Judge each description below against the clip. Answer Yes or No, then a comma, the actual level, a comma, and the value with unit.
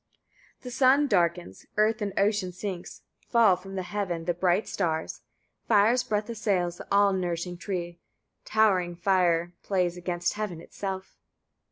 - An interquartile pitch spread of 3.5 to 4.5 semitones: No, average, 3.1 semitones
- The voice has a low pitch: No, high, 190 Hz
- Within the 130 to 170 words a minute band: Yes, average, 140 wpm